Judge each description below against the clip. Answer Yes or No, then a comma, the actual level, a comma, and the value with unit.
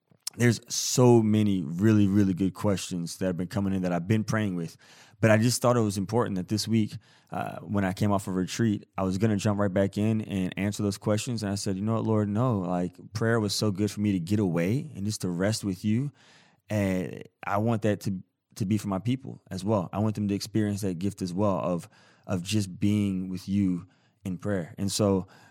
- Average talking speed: No, fast, 240 wpm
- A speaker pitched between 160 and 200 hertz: No, low, 105 Hz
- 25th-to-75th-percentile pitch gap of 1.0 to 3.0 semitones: Yes, narrow, 2.5 semitones